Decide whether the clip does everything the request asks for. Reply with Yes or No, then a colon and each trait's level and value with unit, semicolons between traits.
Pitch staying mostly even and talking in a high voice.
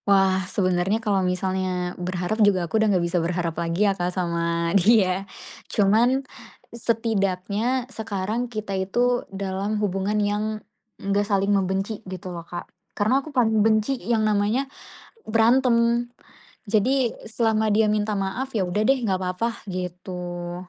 No: average, 3.3 semitones; high, 200 Hz